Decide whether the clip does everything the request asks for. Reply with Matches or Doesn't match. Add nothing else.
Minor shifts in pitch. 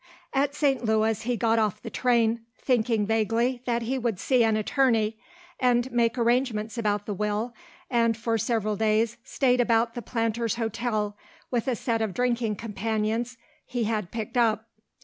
Matches